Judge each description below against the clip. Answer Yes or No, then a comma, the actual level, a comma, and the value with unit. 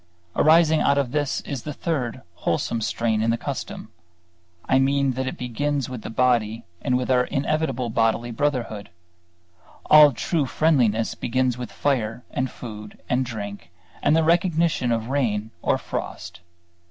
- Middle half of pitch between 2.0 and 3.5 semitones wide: No, average, 4.0 semitones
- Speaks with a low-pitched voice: Yes, low, 125 Hz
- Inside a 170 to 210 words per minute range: No, average, 155 wpm